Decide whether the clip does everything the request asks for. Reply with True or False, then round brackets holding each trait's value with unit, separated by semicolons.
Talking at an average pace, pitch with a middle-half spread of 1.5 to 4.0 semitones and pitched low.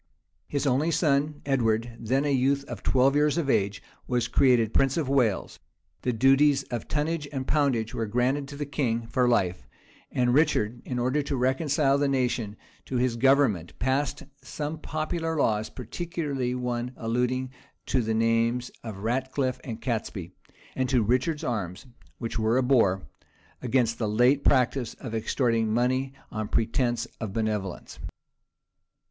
True (155 wpm; 3.3 semitones; 125 Hz)